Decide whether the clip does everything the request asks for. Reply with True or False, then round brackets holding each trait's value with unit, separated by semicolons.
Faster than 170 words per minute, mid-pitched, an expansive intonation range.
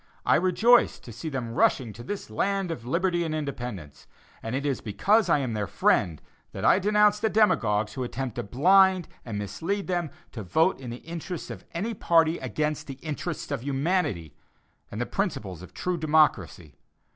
True (180 wpm; 150 Hz; 7.8 semitones)